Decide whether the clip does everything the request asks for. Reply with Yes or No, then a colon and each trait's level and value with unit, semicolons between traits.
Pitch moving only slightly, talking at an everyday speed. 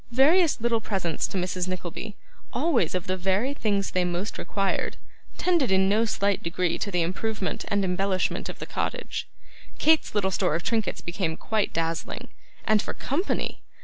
No: average, 3.7 semitones; average, 165 wpm